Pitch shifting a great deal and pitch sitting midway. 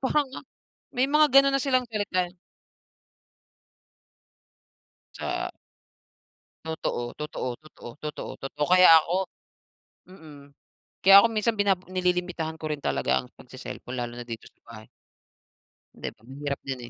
Yes: wide, 6.8 semitones; medium, 165 Hz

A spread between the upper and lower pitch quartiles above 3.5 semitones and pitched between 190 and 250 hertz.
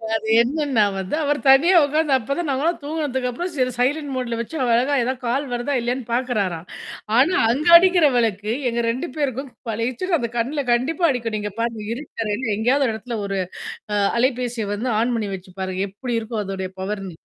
Yes: average, 4.2 semitones; high, 245 Hz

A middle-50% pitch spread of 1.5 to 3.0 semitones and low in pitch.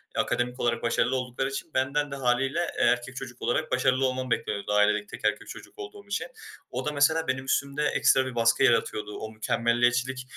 Yes: narrow, 2.4 semitones; low, 130 Hz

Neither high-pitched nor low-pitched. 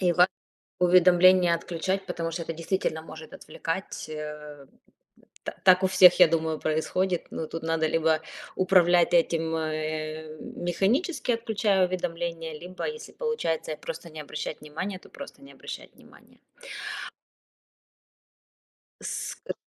Yes: medium, 170 Hz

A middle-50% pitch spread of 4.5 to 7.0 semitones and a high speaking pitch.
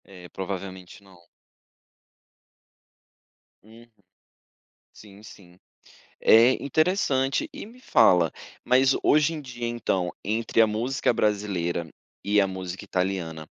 No: average, 5.0 semitones; low, 105 Hz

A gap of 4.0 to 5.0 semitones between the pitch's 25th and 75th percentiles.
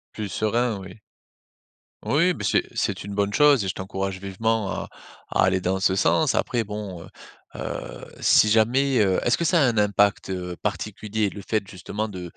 No: average, 2.9 semitones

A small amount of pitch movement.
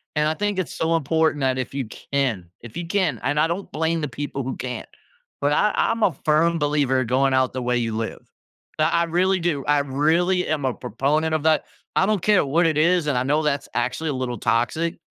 No: average, 4.1 semitones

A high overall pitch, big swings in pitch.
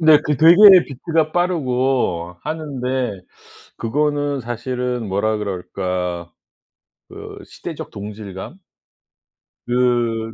No: low, 125 Hz; wide, 5.9 semitones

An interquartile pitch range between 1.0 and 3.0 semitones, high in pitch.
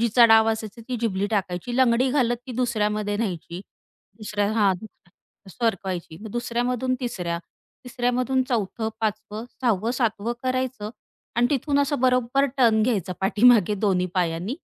No: average, 3.4 semitones; high, 225 Hz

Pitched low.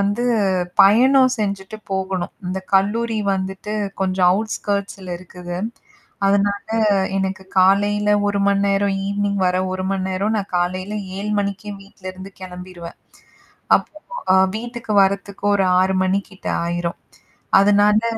No: high, 195 Hz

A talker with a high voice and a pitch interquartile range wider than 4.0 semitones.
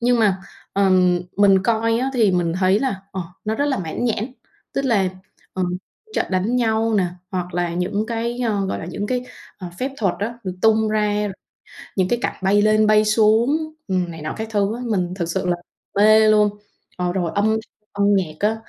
No: high, 210 Hz; average, 3.2 semitones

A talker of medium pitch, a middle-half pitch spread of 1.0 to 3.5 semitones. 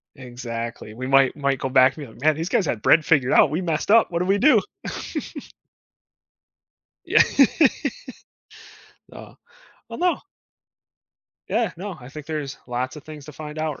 No: medium, 150 Hz; average, 4.0 semitones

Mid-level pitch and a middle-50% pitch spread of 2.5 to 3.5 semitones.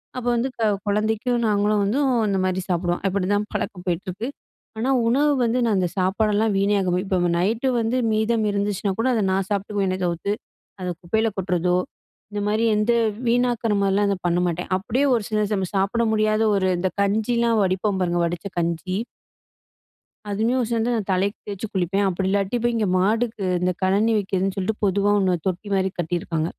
No: high, 200 Hz; average, 2.9 semitones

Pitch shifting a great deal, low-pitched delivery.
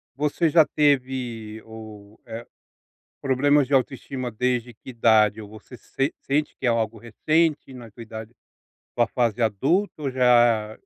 No: average, 3.5 semitones; low, 120 Hz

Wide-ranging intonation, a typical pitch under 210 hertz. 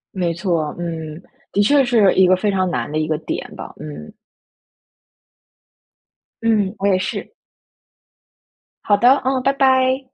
Yes: wide, 6.6 semitones; high, 190 Hz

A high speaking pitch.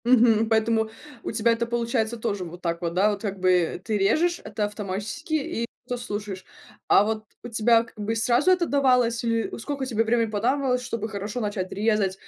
Yes: high, 225 Hz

